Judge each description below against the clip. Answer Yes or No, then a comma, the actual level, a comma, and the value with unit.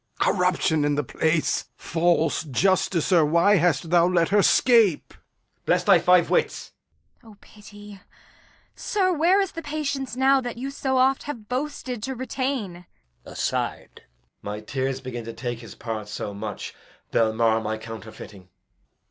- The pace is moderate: Yes, average, 155 wpm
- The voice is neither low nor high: Yes, medium, 180 Hz